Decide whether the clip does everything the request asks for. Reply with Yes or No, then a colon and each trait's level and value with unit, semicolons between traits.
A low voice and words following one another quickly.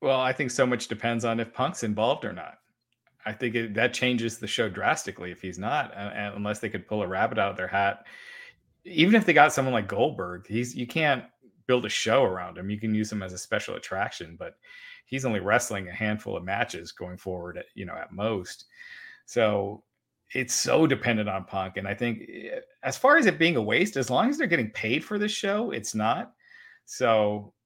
Yes: low, 115 Hz; fast, 215 wpm